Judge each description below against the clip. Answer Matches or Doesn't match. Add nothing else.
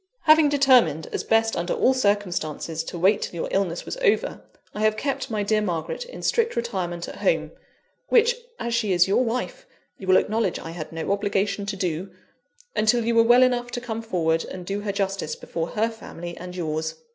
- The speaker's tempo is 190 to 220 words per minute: Matches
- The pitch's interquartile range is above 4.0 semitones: Matches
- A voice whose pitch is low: Doesn't match